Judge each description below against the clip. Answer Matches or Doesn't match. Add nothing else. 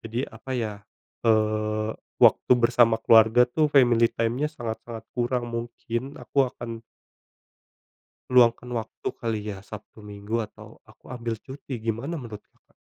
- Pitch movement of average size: Doesn't match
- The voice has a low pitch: Matches